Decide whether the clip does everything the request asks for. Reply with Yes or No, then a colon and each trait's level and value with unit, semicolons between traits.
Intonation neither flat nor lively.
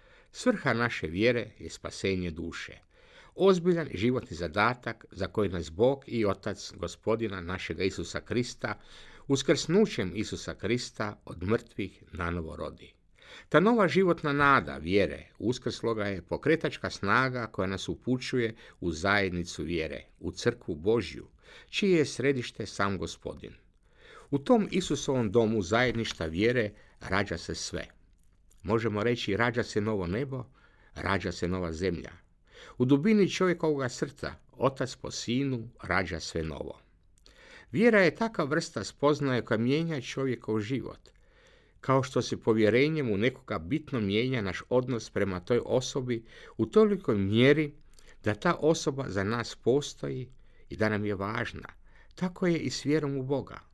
No: wide, 6.0 semitones